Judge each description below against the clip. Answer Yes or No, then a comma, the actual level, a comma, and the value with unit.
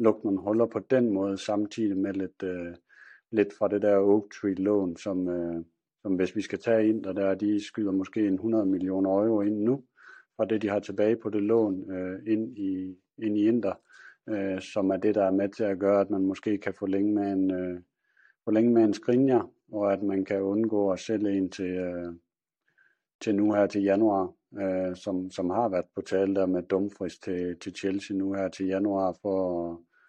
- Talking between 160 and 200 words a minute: No, average, 210 wpm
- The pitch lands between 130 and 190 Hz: No, low, 100 Hz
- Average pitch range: No, narrow, 1.9 semitones